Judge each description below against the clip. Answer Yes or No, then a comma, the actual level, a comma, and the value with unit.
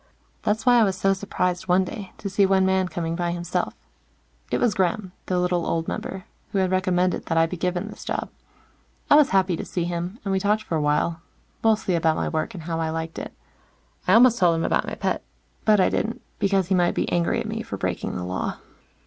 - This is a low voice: No, medium, 185 Hz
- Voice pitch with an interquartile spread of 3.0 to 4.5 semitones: No, narrow, 2.4 semitones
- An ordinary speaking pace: No, fast, 230 wpm